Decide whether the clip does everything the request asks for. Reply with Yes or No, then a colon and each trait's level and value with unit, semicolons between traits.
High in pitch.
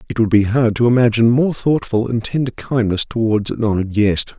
No: low, 115 Hz